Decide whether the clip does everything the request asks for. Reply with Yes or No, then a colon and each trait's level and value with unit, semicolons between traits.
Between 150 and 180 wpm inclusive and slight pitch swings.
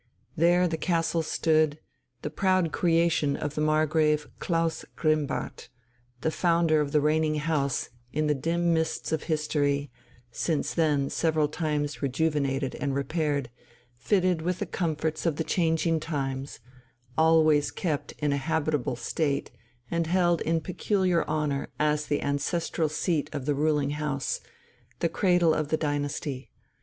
No: average, 140 wpm; narrow, 2.2 semitones